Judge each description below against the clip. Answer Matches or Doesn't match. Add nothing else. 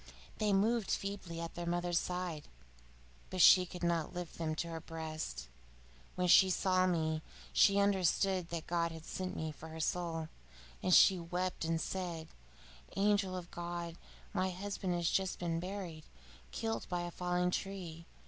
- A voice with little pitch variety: Matches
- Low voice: Doesn't match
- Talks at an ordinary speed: Matches